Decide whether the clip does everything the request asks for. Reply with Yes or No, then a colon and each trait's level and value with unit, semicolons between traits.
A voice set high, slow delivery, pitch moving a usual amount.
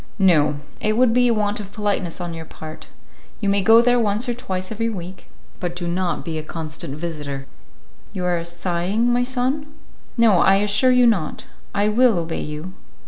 No: high, 195 Hz; average, 190 wpm; average, 5.0 semitones